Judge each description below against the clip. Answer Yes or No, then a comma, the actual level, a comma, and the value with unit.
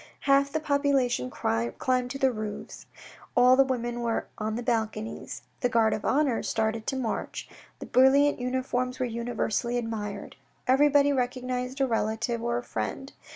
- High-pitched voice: Yes, high, 245 Hz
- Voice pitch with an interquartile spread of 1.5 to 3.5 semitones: Yes, average, 2.9 semitones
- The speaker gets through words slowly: No, average, 155 wpm